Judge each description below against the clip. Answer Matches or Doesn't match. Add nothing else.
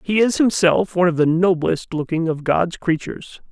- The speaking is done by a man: Matches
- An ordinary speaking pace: Matches